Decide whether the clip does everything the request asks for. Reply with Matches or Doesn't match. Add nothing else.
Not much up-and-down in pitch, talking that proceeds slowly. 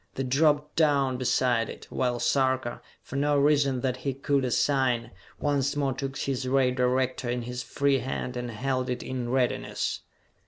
Doesn't match